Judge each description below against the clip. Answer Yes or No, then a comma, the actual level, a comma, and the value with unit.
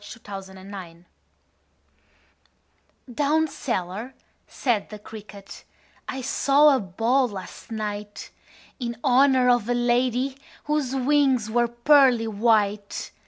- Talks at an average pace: No, slow, 110 wpm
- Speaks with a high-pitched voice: Yes, high, 240 Hz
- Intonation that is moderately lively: Yes, average, 4.3 semitones